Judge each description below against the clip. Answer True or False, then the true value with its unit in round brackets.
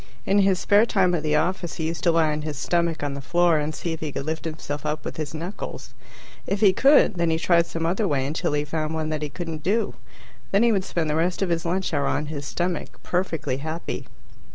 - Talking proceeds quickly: True (245 wpm)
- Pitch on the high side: False (165 Hz)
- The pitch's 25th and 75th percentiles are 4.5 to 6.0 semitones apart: False (2.9 semitones)